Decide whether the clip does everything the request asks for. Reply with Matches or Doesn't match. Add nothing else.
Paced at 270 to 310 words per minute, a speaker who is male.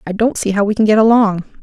Doesn't match